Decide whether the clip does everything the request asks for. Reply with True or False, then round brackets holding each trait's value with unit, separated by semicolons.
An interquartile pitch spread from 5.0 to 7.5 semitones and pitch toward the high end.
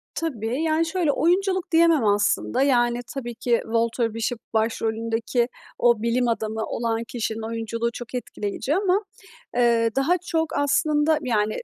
True (5.4 semitones; 240 Hz)